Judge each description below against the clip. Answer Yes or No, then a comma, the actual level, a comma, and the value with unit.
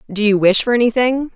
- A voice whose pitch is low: No, high, 225 Hz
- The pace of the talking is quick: Yes, fast, 220 wpm